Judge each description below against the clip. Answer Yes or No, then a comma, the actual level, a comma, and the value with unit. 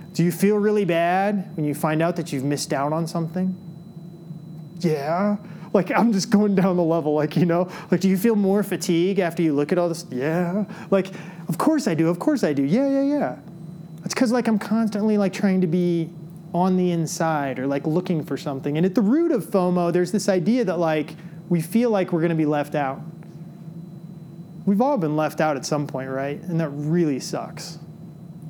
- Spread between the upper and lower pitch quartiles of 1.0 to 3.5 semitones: Yes, average, 3.0 semitones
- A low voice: No, medium, 170 Hz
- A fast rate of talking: Yes, fast, 215 wpm